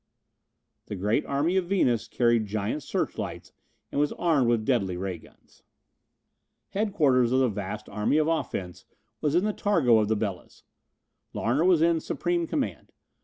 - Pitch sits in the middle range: No, low, 130 Hz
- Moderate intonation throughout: No, wide, 7.5 semitones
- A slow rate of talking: No, average, 155 wpm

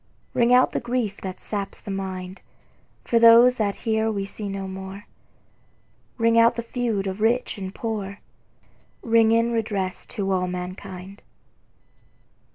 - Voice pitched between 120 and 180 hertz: No, high, 205 Hz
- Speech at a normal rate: Yes, average, 145 wpm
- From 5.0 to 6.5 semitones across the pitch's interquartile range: No, average, 3.1 semitones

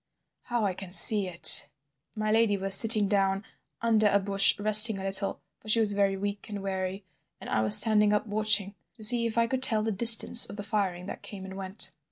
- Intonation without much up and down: Yes, narrow, 1.9 semitones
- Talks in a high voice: Yes, high, 205 Hz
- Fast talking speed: Yes, fast, 220 wpm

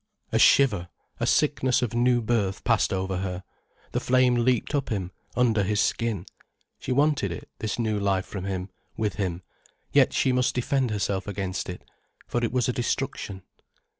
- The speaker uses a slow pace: No, average, 170 wpm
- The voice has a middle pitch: No, low, 110 Hz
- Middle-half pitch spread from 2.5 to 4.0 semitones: No, average, 4.6 semitones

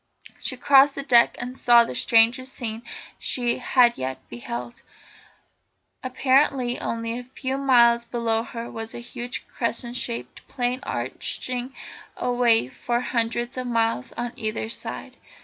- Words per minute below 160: Yes, slow, 135 wpm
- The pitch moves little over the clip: Yes, narrow, 1.7 semitones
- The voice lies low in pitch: No, high, 240 Hz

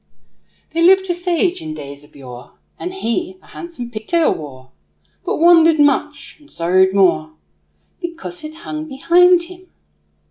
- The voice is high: Yes, very high, 305 Hz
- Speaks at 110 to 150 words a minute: Yes, average, 145 wpm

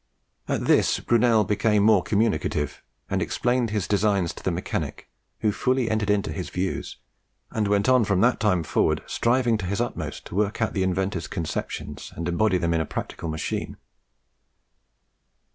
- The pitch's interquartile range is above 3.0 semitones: Yes, average, 3.6 semitones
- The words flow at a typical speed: Yes, average, 165 wpm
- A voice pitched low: Yes, low, 105 Hz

